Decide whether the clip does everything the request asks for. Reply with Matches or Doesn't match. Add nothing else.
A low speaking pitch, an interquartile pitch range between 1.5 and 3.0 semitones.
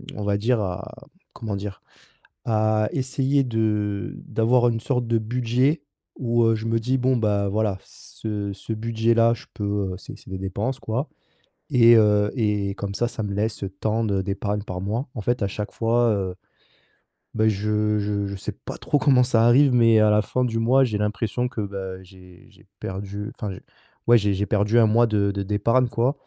Matches